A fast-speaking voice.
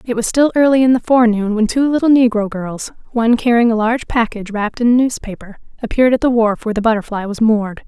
Yes: fast, 230 wpm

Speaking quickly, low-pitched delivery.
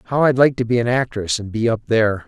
Yes: fast, 315 wpm; low, 115 Hz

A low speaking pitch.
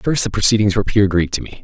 Yes: low, 105 Hz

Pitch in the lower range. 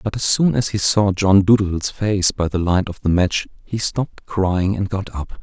Yes: low, 100 Hz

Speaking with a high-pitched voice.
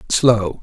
No: low, 110 Hz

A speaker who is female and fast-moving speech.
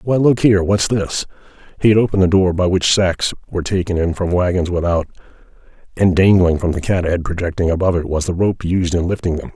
No: male; fast, 220 wpm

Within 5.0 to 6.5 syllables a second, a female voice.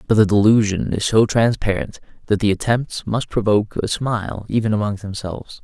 No: 5.5 syllables/s; male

